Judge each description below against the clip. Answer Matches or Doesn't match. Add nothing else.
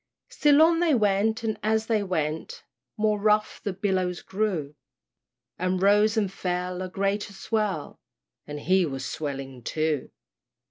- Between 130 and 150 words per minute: Matches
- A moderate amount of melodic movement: Matches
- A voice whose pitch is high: Matches